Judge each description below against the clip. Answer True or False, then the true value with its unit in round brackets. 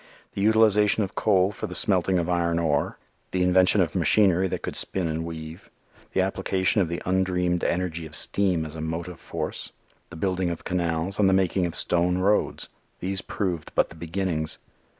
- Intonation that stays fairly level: True (2.2 semitones)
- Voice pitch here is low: True (90 Hz)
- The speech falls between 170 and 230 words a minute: True (185 wpm)